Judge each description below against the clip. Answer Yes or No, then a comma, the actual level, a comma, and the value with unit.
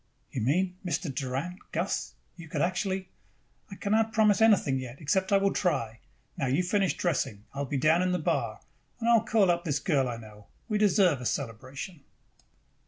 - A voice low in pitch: No, medium, 170 Hz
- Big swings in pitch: Yes, wide, 6.2 semitones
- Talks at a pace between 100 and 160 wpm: No, average, 200 wpm